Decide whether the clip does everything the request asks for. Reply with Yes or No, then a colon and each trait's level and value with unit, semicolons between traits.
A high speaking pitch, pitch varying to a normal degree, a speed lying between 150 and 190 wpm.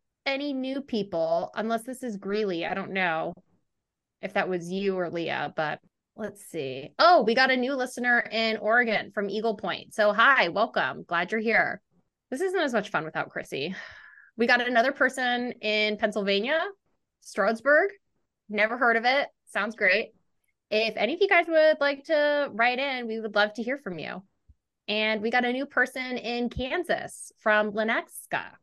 Yes: high, 225 Hz; average, 4.0 semitones; average, 175 wpm